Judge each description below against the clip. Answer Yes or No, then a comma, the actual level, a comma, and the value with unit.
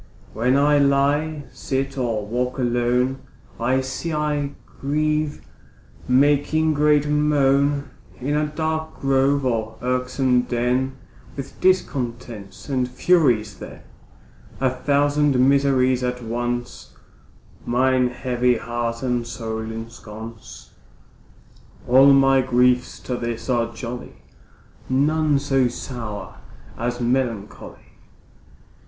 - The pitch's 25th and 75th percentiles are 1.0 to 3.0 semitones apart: Yes, average, 2.7 semitones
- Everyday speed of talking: No, slow, 100 wpm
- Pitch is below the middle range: Yes, low, 130 Hz